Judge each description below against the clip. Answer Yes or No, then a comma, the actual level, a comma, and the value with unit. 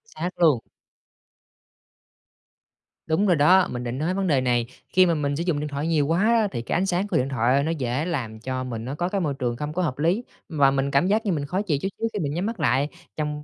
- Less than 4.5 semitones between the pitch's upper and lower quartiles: No, average, 5.0 semitones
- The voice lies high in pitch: No, medium, 150 Hz